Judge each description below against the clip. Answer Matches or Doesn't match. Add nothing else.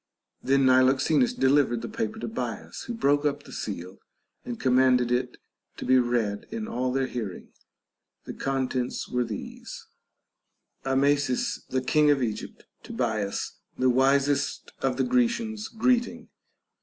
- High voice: Doesn't match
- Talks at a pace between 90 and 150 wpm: Matches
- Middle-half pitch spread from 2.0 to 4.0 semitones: Matches